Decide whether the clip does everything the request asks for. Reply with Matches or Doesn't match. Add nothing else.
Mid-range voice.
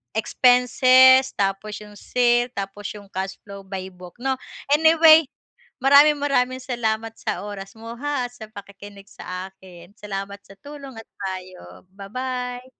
Doesn't match